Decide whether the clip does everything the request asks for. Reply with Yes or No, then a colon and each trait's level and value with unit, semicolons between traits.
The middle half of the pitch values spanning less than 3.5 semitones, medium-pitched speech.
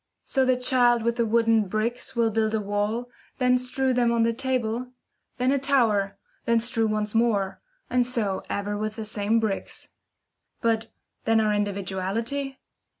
No: average, 2.7 semitones; high, 230 Hz